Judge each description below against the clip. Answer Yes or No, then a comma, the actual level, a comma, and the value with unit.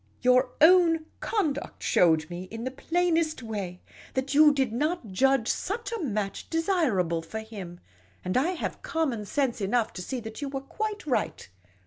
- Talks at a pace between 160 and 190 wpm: Yes, average, 165 wpm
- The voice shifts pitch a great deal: Yes, wide, 7.3 semitones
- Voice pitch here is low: No, very high, 260 Hz